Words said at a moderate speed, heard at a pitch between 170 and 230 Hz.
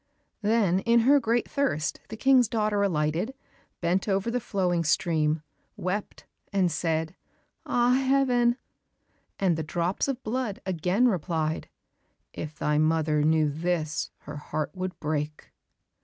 No: slow, 130 wpm; medium, 185 Hz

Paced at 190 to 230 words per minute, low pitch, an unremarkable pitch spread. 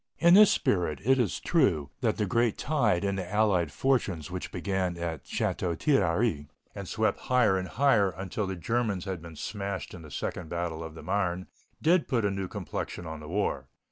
Yes: average, 195 wpm; very low, 95 Hz; average, 4.8 semitones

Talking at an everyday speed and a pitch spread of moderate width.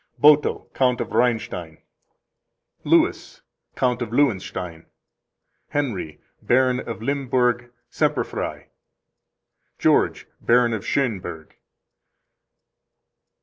No: slow, 75 wpm; average, 4.8 semitones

